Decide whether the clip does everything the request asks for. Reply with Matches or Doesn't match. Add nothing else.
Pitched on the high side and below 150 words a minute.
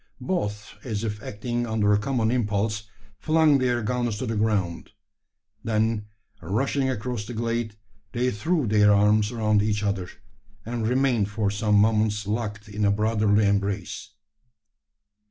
Doesn't match